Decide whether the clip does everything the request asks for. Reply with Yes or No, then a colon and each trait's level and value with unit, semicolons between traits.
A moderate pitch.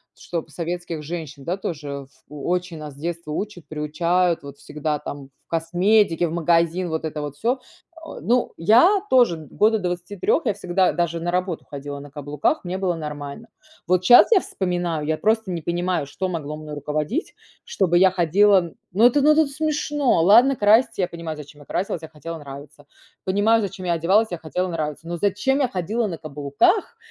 Yes: medium, 175 Hz